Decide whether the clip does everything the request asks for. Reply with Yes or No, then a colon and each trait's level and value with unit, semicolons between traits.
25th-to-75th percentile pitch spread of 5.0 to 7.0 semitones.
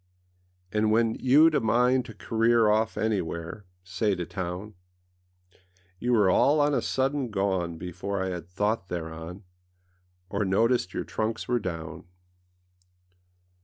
No: average, 4.3 semitones